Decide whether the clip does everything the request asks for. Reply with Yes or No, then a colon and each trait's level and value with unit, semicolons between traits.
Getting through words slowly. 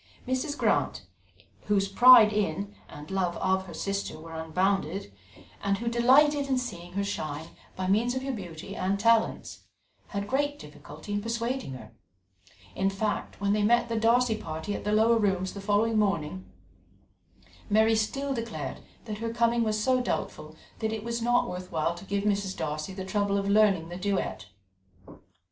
No: average, 170 wpm